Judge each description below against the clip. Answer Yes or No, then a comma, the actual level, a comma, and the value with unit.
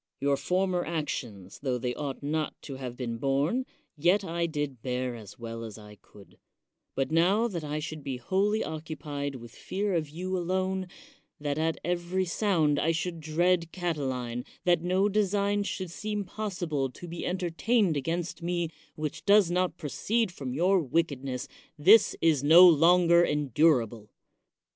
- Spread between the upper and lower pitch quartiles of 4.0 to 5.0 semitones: Yes, average, 4.7 semitones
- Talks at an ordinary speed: Yes, average, 160 wpm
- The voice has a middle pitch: Yes, medium, 165 Hz